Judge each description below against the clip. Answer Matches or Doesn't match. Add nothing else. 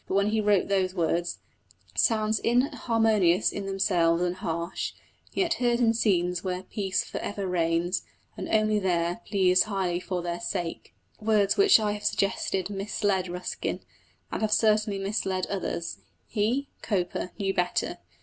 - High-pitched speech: Matches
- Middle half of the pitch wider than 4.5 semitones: Doesn't match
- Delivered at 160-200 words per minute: Doesn't match